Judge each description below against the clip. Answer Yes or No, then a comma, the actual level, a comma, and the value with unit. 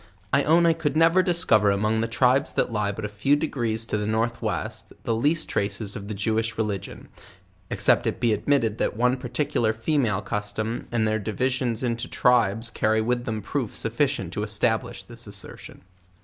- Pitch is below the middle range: Yes, low, 115 Hz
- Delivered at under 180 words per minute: No, average, 185 wpm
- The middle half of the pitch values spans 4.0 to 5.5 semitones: No, average, 3.2 semitones